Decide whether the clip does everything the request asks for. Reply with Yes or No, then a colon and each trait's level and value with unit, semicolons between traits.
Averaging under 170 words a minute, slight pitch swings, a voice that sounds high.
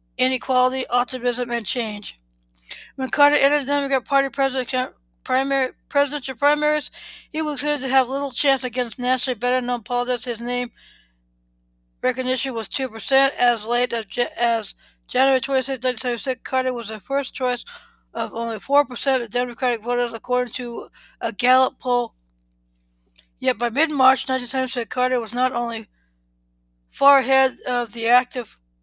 Yes: average, 140 wpm; narrow, 2.3 semitones; very high, 250 Hz